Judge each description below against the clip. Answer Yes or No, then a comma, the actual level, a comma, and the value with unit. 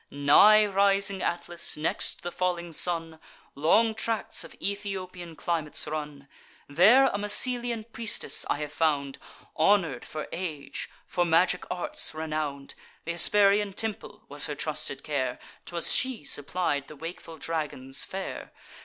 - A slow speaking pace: Yes, slow, 130 wpm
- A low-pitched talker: No, medium, 170 Hz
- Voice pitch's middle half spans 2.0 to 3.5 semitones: No, average, 5.0 semitones